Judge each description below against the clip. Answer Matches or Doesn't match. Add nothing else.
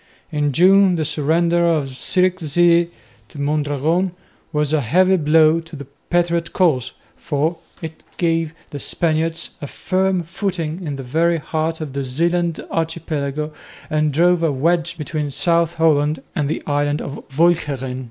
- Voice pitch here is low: Doesn't match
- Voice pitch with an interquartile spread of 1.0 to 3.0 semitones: Matches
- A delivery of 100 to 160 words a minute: Matches